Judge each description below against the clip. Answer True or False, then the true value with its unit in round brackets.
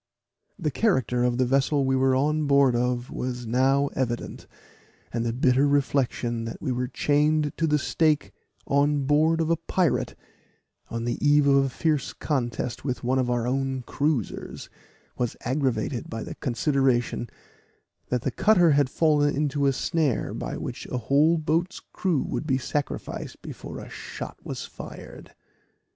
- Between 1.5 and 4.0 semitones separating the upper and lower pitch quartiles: True (3.1 semitones)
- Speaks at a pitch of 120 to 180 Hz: True (135 Hz)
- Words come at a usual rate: True (160 wpm)